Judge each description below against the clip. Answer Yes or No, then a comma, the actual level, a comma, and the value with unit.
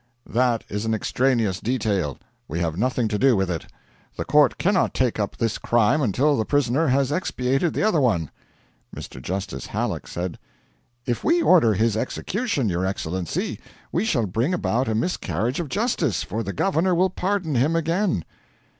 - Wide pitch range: Yes, wide, 7.7 semitones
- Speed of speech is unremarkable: Yes, average, 170 wpm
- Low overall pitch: Yes, low, 125 Hz